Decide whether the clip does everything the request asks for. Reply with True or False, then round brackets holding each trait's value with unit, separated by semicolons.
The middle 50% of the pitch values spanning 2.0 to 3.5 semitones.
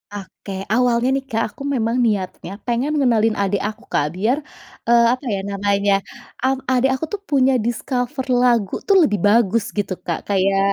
False (4.0 semitones)